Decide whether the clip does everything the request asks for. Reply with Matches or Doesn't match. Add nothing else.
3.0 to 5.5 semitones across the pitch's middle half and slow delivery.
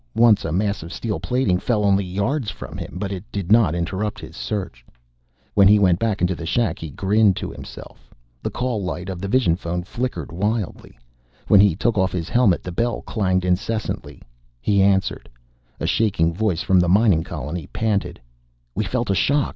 Doesn't match